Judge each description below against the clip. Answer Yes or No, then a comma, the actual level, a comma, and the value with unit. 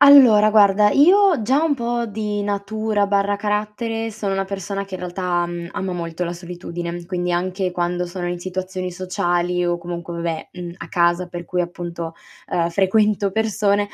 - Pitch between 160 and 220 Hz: Yes, medium, 185 Hz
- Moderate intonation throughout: Yes, average, 3.1 semitones